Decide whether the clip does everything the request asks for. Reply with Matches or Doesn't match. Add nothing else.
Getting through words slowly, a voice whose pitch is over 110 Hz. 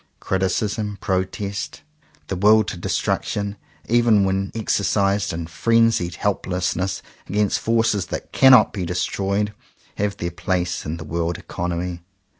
Doesn't match